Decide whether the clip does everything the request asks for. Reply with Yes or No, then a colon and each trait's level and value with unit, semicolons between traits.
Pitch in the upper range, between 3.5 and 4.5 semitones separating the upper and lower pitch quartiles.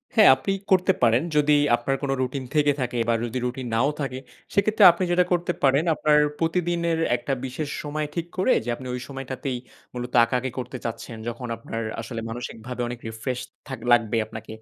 No: low, 130 Hz; average, 4.1 semitones